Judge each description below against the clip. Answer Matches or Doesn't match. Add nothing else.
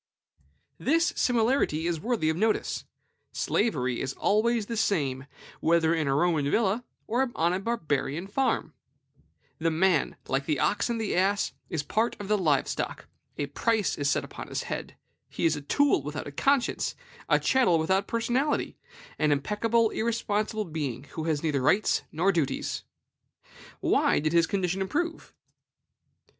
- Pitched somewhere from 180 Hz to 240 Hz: Matches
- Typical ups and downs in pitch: Doesn't match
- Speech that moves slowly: Doesn't match